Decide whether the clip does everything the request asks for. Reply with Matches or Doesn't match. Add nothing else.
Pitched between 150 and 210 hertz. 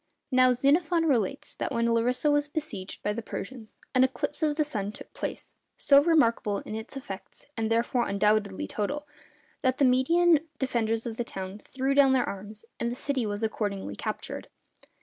Doesn't match